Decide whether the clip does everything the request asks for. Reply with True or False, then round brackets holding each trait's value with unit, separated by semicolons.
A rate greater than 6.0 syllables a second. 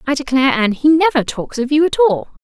True (6.2 syllables/s)